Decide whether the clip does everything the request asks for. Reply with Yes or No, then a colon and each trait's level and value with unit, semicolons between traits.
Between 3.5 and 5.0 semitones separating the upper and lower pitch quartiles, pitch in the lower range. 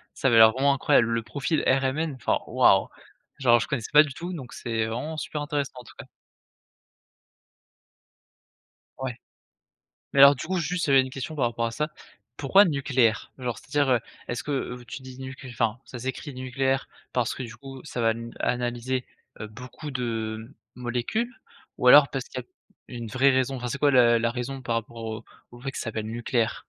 No: average, 2.8 semitones; low, 130 Hz